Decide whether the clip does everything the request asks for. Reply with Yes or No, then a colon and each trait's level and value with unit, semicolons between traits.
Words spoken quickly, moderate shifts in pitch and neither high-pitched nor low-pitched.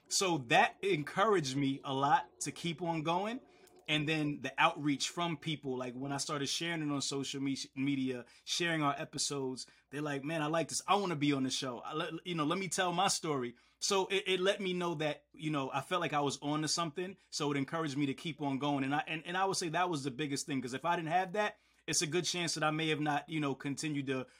Yes: fast, 265 wpm; average, 3.7 semitones; medium, 155 Hz